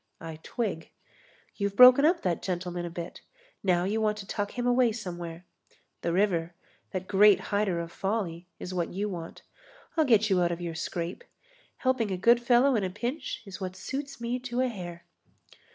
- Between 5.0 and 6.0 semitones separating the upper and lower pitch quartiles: Yes, average, 5.3 semitones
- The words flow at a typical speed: Yes, average, 185 wpm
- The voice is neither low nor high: No, high, 195 Hz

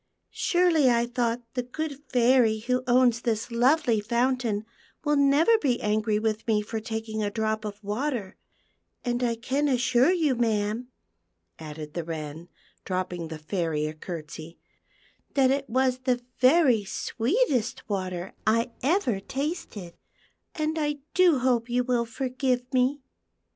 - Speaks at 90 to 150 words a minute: Yes, average, 145 wpm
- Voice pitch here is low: No, high, 240 Hz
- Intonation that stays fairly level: No, average, 3.9 semitones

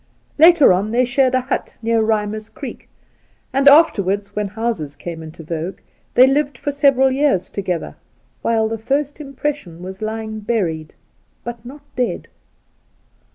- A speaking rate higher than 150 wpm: No, average, 145 wpm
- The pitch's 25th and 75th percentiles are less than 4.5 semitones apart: No, wide, 5.5 semitones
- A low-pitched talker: No, high, 225 Hz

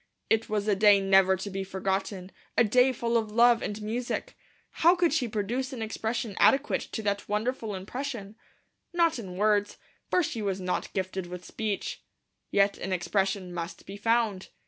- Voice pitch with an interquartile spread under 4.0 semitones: Yes, average, 3.5 semitones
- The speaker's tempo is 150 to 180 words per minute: Yes, average, 170 wpm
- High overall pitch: Yes, high, 210 Hz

